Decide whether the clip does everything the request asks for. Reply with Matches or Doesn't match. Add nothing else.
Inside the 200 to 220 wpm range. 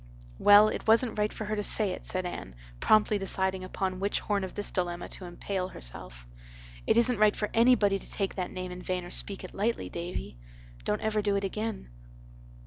Matches